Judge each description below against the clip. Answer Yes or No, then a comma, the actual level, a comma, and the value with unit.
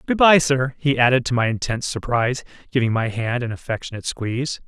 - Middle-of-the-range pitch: No, low, 125 Hz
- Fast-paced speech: No, average, 190 wpm